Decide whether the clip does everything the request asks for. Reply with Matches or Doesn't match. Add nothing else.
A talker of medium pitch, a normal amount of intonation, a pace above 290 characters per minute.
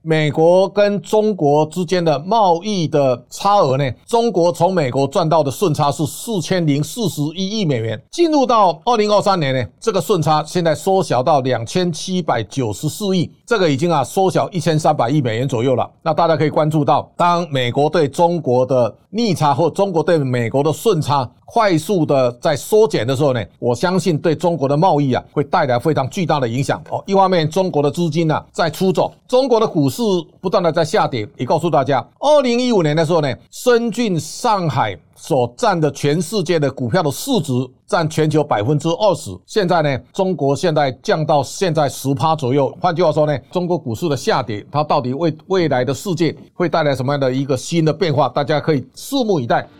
Matches